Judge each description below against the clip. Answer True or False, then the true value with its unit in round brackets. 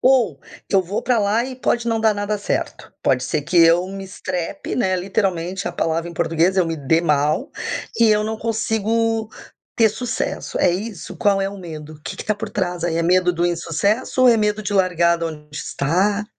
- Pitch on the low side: False (190 Hz)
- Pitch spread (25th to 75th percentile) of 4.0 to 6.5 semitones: True (4.4 semitones)